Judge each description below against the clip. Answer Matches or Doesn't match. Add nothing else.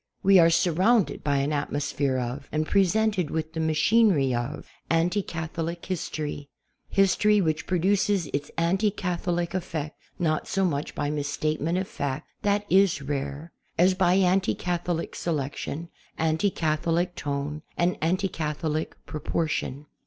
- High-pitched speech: Doesn't match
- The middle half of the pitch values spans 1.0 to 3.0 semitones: Doesn't match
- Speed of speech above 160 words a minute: Doesn't match